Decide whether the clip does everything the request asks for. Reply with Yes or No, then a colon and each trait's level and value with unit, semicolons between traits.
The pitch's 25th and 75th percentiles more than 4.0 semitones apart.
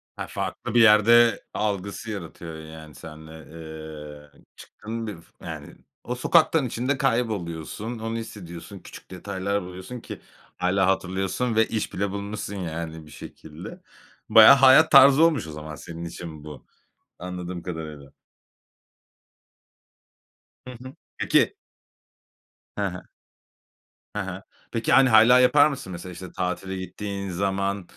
Yes: average, 4.8 semitones